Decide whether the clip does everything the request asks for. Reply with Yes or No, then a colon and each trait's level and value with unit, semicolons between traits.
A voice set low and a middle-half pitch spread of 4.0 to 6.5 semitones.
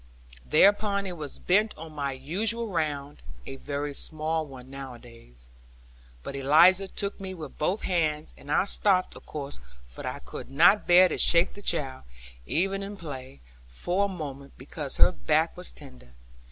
No: medium, 155 Hz; average, 5.2 semitones